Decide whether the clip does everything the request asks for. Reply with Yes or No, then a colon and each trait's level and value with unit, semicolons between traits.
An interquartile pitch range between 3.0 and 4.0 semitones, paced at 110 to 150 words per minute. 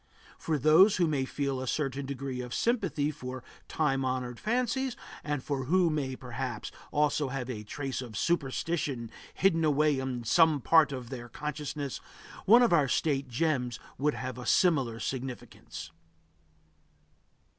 Yes: average, 3.5 semitones; average, 145 wpm